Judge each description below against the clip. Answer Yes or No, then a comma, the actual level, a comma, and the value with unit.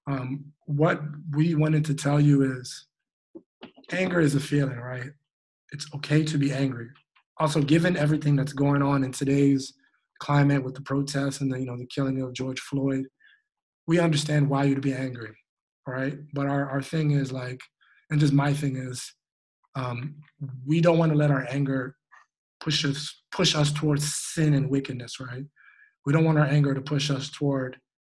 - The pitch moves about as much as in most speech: No, narrow, 1.9 semitones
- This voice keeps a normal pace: Yes, average, 175 wpm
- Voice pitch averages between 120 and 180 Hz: Yes, medium, 140 Hz